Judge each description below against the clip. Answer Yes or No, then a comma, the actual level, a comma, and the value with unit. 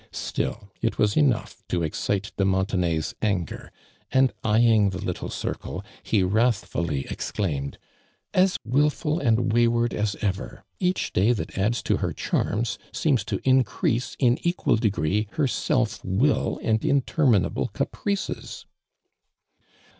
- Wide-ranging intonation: No, average, 4.7 semitones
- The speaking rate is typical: No, slow, 130 wpm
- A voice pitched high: No, low, 110 Hz